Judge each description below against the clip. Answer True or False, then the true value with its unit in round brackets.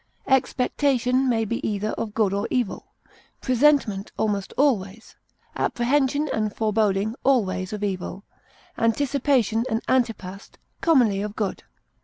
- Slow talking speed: True (115 wpm)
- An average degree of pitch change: True (4.3 semitones)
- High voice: True (225 Hz)